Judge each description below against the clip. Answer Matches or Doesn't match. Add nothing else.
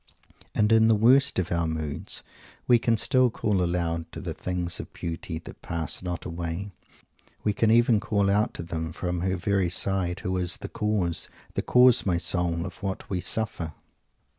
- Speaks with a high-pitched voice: Doesn't match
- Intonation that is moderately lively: Matches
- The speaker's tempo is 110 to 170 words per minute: Doesn't match